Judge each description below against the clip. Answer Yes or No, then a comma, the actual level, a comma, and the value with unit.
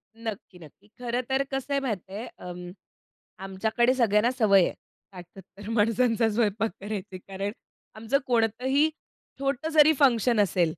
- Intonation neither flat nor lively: Yes, average, 4.2 semitones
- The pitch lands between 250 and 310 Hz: No, high, 220 Hz